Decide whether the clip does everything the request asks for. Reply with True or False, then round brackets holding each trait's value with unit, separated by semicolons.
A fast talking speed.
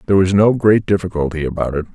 True (215 wpm)